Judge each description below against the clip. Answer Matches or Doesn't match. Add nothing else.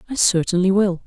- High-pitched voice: Matches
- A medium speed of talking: Matches